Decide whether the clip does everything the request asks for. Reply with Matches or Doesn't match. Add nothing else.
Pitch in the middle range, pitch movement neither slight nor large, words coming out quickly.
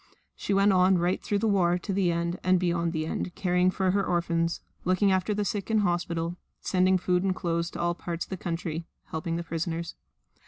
Doesn't match